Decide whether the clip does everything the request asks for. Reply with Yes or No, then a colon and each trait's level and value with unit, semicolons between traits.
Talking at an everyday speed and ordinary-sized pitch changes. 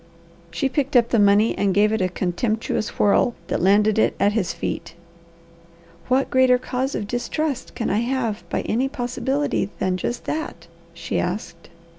Yes: average, 165 wpm; average, 4.3 semitones